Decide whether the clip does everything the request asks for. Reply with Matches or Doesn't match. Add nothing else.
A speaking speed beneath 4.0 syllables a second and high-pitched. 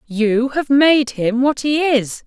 Matches